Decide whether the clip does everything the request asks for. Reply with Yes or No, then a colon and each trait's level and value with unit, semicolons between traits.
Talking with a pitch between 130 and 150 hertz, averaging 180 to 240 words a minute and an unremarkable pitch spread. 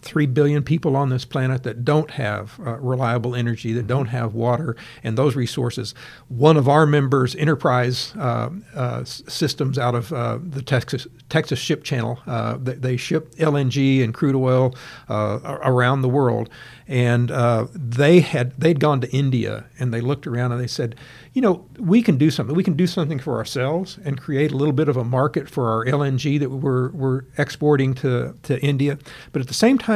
Yes: low, 135 Hz; average, 195 wpm; average, 3.3 semitones